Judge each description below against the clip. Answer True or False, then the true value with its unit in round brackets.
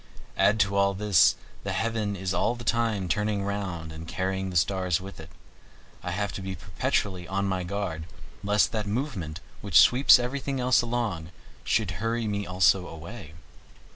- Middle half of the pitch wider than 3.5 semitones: False (3.2 semitones)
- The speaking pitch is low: True (100 Hz)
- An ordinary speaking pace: True (170 wpm)